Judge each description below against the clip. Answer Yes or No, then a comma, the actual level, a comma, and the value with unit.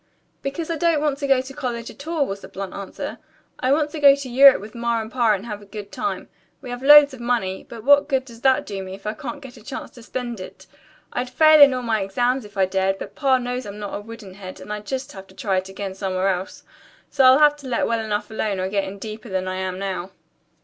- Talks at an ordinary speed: No, fast, 270 wpm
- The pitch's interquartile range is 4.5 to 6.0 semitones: Yes, average, 5.2 semitones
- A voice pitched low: No, high, 230 Hz